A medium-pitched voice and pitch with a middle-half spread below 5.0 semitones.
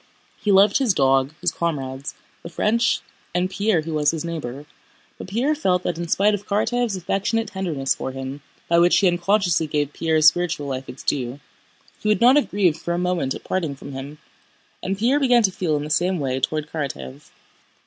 No: medium, 170 Hz; wide, 5.4 semitones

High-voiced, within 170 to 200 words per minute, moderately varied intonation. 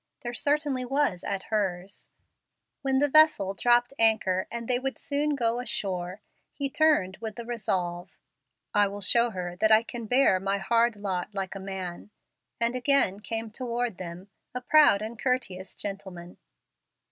No: high, 220 Hz; average, 160 wpm; average, 4.6 semitones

